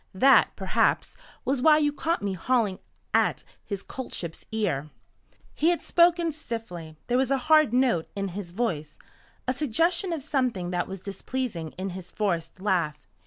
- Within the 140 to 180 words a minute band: Yes, average, 160 wpm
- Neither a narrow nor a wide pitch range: No, wide, 7.2 semitones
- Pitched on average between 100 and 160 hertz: No, high, 225 Hz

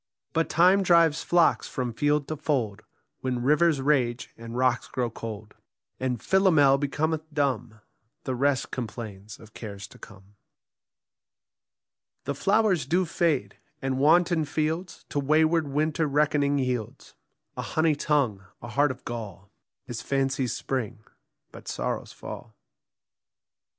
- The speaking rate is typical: No, slow, 130 wpm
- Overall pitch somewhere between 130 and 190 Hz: Yes, medium, 140 Hz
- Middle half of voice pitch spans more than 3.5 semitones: Yes, average, 4.6 semitones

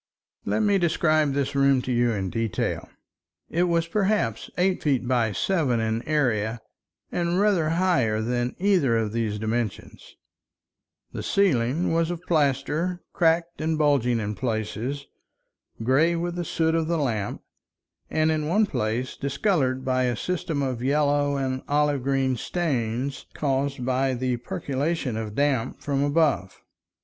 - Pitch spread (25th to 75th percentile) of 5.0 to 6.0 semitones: Yes, average, 5.3 semitones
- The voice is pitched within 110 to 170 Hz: Yes, medium, 140 Hz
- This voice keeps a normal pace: Yes, average, 145 wpm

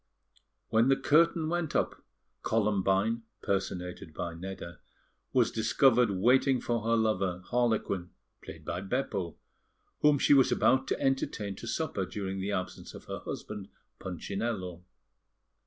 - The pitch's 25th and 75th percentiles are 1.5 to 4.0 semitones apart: No, average, 4.8 semitones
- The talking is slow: Yes, slow, 130 wpm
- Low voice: Yes, low, 110 Hz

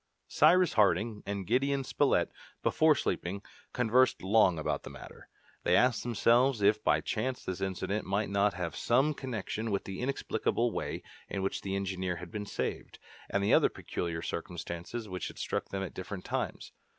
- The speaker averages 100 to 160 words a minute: No, average, 170 wpm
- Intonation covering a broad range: No, average, 4.1 semitones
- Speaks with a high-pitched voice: No, low, 100 Hz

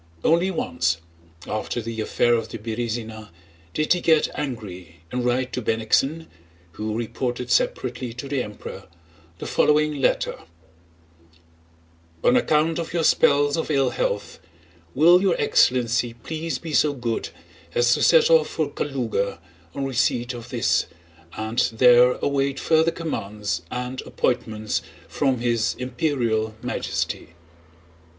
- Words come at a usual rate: No, slow, 130 wpm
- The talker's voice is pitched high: No, low, 125 Hz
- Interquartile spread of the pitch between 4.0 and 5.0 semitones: Yes, average, 4.5 semitones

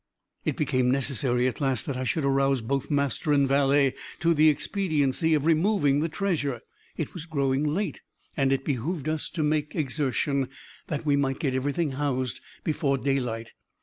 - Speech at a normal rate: Yes, average, 170 wpm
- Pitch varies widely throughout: No, narrow, 2.6 semitones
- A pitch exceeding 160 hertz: No, medium, 140 Hz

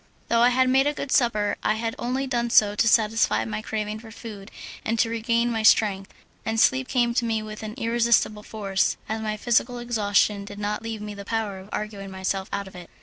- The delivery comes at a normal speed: No, fast, 220 wpm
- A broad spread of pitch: No, narrow, 2.4 semitones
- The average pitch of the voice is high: Yes, high, 220 Hz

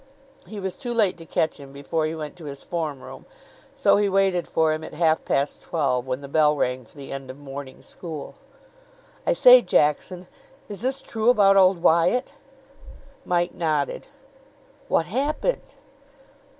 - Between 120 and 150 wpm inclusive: No, average, 165 wpm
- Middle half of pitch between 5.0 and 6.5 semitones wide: Yes, wide, 5.4 semitones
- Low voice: No, medium, 165 Hz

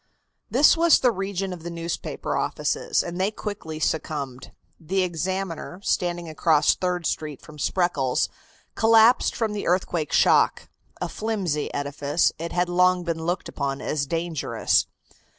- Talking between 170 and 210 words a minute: No, average, 140 wpm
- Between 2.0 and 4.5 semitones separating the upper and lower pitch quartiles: Yes, average, 3.6 semitones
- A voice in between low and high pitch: Yes, medium, 175 Hz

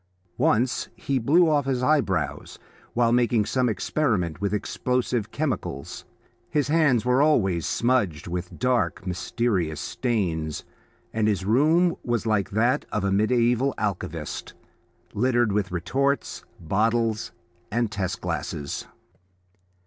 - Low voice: Yes, low, 115 Hz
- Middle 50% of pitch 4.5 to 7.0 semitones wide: Yes, average, 4.8 semitones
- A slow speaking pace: Yes, slow, 120 wpm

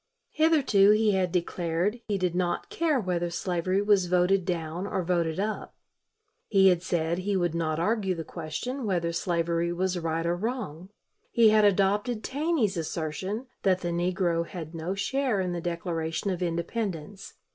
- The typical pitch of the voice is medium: Yes, medium, 180 Hz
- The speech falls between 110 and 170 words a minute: Yes, average, 160 wpm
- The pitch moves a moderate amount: Yes, average, 3.3 semitones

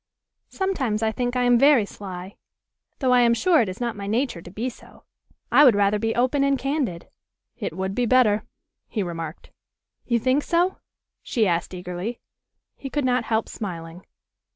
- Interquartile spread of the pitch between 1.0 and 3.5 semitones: No, average, 4.9 semitones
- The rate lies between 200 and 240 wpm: No, average, 175 wpm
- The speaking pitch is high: Yes, high, 230 Hz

